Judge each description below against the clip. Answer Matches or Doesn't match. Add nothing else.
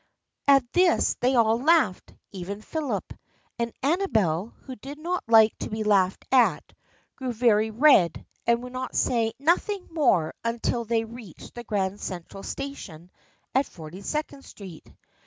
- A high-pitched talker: Matches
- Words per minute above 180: Doesn't match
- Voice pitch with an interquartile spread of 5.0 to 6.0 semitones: Matches